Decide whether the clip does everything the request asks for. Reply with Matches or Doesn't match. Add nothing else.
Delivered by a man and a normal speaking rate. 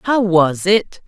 Doesn't match